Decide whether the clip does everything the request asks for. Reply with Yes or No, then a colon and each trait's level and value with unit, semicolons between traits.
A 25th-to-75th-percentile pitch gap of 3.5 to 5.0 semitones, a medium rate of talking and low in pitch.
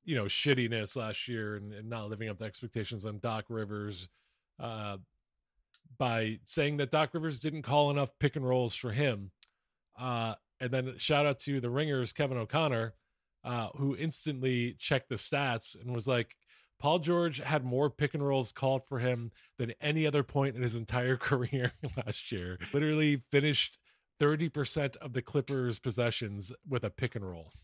Yes: average, 4.2 semitones; average, 175 wpm; low, 125 Hz